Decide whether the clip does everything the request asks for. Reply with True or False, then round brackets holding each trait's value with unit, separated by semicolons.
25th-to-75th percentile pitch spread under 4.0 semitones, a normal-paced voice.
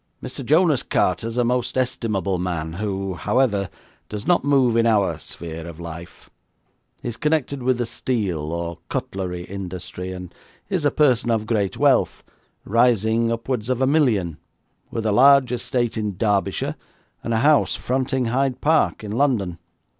False (5.5 semitones; 160 wpm)